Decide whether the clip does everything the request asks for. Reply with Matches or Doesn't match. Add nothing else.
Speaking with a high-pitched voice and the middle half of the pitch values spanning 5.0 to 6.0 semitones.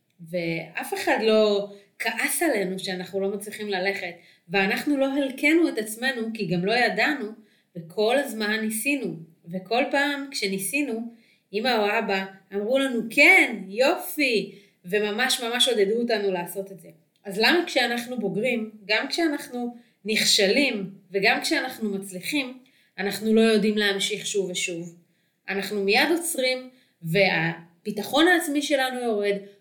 Doesn't match